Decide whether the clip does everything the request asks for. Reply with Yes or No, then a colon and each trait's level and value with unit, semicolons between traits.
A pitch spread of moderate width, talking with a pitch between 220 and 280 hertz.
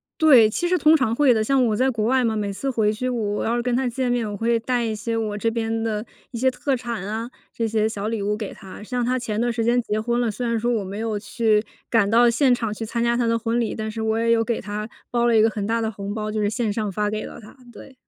No: narrow, 2.0 semitones; high, 225 Hz